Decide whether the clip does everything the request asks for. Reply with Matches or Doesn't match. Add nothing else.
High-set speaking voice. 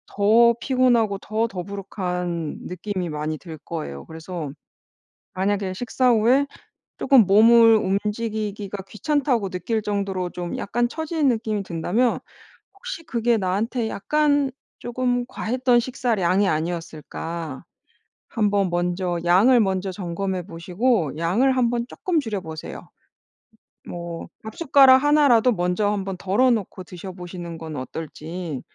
Matches